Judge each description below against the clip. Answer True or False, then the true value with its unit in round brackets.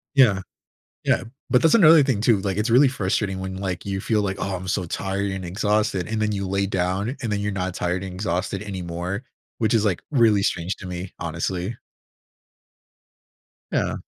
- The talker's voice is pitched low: True (100 Hz)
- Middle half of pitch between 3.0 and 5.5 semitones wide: False (2.6 semitones)